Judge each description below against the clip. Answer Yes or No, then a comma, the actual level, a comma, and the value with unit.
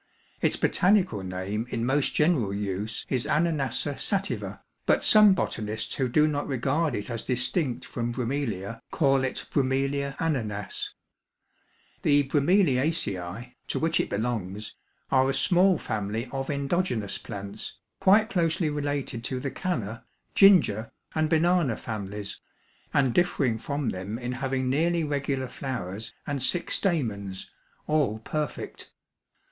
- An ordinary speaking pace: No, slow, 130 wpm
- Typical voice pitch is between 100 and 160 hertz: Yes, low, 135 Hz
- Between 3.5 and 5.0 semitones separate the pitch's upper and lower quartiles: No, wide, 5.6 semitones